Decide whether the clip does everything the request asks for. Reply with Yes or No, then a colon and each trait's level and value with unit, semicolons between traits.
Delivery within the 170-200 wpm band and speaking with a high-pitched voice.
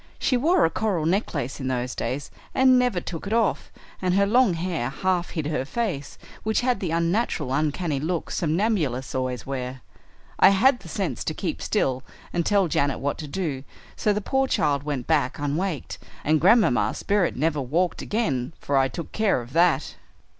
No: average, 180 wpm; medium, 165 Hz